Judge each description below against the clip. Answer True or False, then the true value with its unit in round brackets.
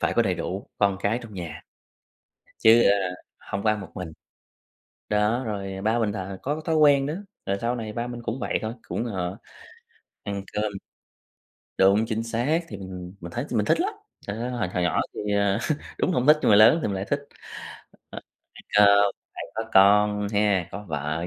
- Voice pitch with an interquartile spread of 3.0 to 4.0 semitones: True (3.3 semitones)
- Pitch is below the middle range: True (105 Hz)